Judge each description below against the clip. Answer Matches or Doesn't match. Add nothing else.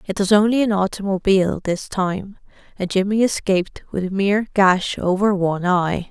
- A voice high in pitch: Matches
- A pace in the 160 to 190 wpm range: Matches